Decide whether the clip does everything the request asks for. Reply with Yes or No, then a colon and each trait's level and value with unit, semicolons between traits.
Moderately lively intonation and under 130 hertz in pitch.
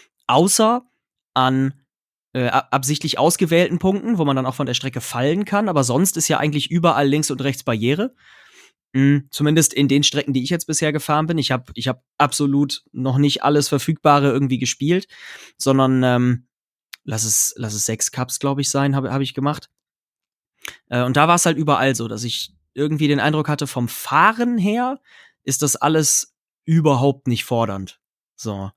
No: average, 3.5 semitones; medium, 140 Hz